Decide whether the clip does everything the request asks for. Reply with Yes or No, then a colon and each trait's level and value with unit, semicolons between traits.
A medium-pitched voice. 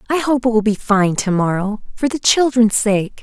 No: high, 225 Hz